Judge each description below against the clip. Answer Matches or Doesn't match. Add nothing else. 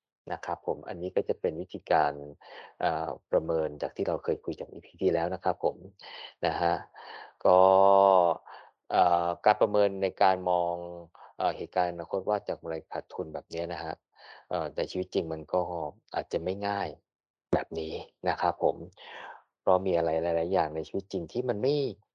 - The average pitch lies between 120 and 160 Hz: Doesn't match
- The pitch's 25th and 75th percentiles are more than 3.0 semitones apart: Doesn't match